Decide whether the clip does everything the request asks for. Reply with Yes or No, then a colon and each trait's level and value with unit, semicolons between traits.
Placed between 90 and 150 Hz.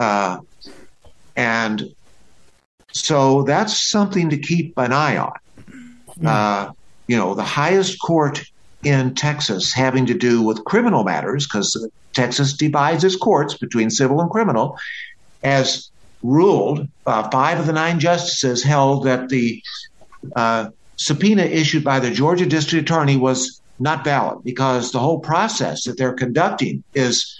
Yes: low, 135 Hz